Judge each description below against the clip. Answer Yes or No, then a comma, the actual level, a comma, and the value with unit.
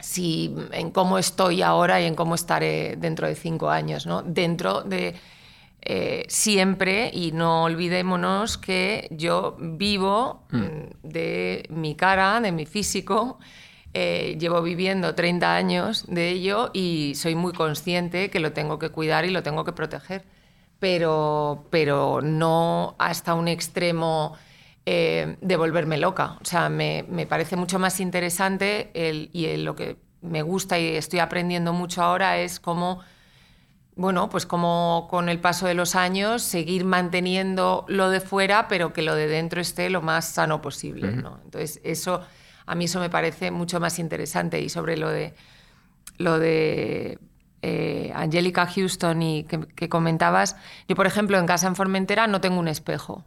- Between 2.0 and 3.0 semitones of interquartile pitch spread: Yes, narrow, 2.6 semitones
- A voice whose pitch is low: No, medium, 175 Hz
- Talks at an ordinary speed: Yes, average, 160 wpm